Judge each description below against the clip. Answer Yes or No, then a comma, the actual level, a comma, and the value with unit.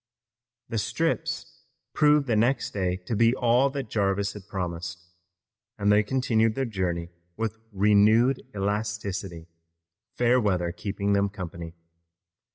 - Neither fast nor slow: No, slow, 125 wpm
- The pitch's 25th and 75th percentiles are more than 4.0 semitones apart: No, average, 3.4 semitones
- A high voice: No, low, 105 Hz